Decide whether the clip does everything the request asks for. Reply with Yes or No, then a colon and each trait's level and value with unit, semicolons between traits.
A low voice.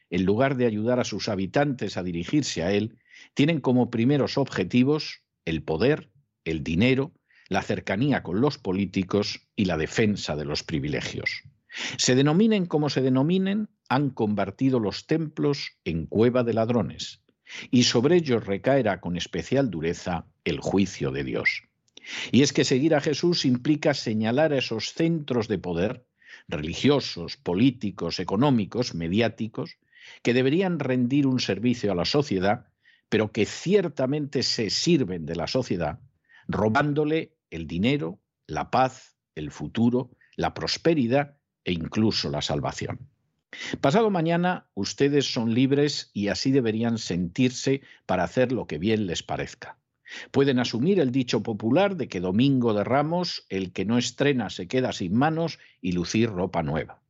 Yes: low, 125 Hz